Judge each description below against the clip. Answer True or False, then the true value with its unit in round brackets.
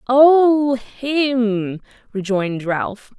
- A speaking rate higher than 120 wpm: False (75 wpm)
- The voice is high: True (240 Hz)